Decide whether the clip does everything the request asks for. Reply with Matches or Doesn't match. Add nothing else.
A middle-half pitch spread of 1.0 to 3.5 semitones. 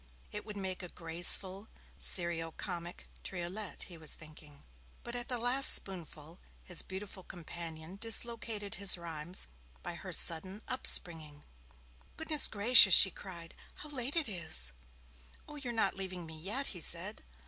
Doesn't match